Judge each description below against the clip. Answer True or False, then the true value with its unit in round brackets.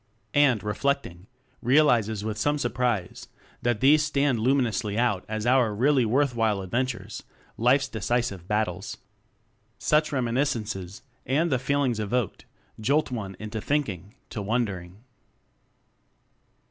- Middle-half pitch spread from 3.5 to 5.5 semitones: True (4.3 semitones)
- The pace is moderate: False (120 wpm)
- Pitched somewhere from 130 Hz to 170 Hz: False (120 Hz)